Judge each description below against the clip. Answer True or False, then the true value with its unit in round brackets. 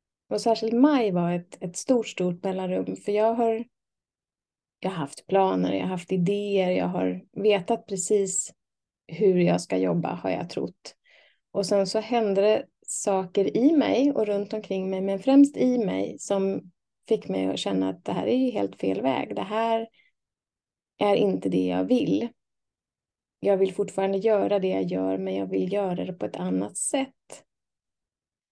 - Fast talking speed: False (175 wpm)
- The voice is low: False (195 Hz)